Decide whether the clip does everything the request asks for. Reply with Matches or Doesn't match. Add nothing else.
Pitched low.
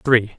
Matches